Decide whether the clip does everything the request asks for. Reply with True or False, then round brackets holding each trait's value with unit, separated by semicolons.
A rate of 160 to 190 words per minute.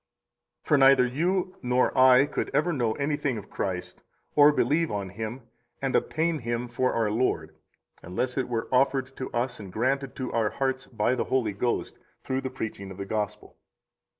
True (180 wpm)